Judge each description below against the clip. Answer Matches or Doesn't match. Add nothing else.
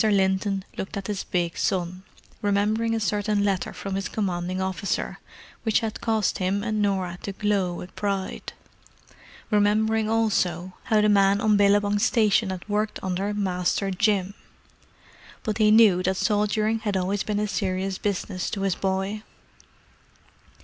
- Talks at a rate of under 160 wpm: Matches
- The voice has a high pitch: Matches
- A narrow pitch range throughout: Matches